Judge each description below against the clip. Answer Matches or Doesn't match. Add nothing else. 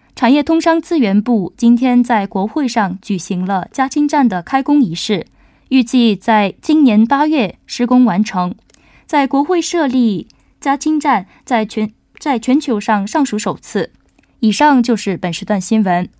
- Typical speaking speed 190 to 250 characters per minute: Matches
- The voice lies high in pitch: Matches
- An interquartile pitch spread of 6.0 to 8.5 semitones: Doesn't match